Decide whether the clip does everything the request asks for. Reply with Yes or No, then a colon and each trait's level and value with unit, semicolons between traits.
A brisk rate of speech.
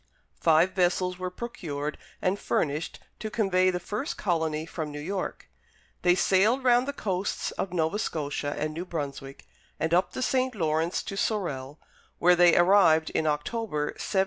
No: average, 160 wpm